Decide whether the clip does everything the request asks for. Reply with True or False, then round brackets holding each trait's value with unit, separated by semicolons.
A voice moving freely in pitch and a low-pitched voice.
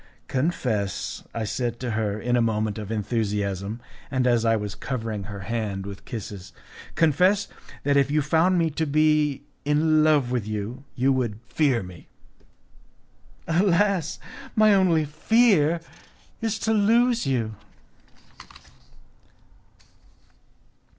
True (6.7 semitones; 130 Hz)